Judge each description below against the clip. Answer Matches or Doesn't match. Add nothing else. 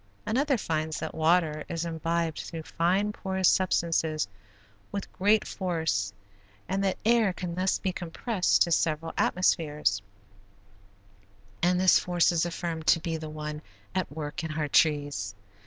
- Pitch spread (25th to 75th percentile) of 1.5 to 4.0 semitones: Matches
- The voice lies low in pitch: Doesn't match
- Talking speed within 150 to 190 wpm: Doesn't match